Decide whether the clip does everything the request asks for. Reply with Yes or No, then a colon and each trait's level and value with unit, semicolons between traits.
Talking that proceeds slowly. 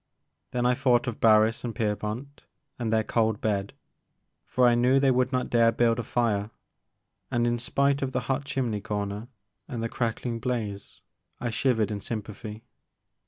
No: average, 165 wpm